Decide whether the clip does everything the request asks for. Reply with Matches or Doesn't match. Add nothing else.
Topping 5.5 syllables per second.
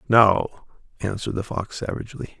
Matches